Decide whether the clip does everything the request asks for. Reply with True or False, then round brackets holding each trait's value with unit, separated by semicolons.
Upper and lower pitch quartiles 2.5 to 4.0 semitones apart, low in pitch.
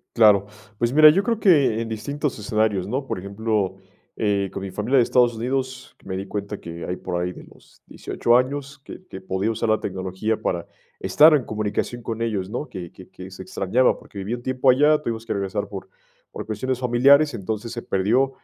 False (4.8 semitones; 110 Hz)